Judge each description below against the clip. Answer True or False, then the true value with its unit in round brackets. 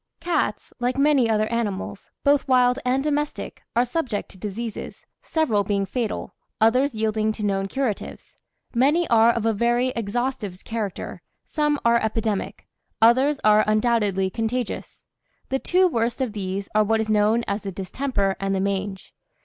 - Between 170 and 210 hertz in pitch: False (225 Hz)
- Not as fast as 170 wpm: True (155 wpm)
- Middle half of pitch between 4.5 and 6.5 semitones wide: False (3.7 semitones)